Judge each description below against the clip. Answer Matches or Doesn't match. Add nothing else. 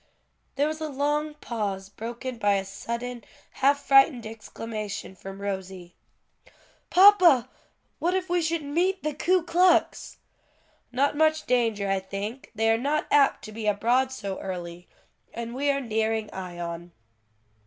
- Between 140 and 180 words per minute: Matches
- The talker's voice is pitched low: Doesn't match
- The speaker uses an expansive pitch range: Matches